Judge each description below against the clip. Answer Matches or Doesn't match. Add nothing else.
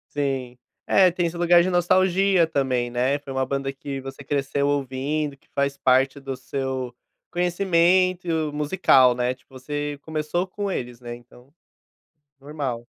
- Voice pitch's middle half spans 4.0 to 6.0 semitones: Matches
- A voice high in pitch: Doesn't match